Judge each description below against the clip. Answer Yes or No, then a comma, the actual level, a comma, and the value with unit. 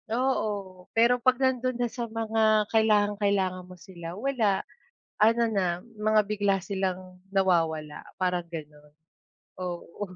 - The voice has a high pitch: Yes, high, 200 Hz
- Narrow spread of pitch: No, average, 3.6 semitones